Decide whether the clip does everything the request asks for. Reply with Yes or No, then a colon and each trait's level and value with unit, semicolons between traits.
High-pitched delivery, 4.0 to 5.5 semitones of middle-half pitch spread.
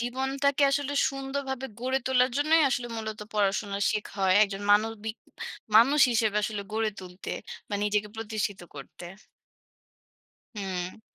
Yes: high, 220 Hz; average, 4.4 semitones